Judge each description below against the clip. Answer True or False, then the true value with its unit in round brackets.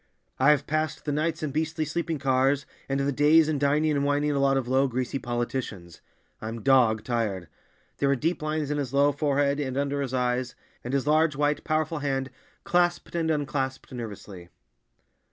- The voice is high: False (140 Hz)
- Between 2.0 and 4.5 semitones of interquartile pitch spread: True (2.7 semitones)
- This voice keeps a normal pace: True (175 wpm)